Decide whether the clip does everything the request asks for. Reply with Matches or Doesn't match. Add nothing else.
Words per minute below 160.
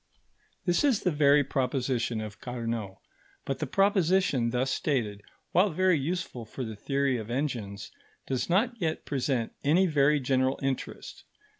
Matches